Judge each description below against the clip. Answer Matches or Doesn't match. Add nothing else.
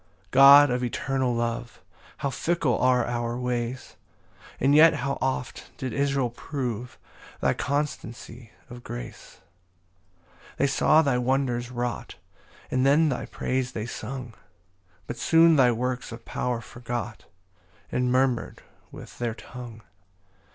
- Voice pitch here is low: Matches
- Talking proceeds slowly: Matches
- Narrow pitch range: Matches